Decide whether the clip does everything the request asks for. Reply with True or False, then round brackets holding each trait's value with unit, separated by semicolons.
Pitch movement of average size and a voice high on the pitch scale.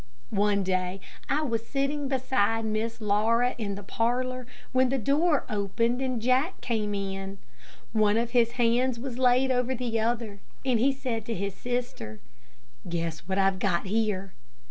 True (3.9 semitones; 230 Hz)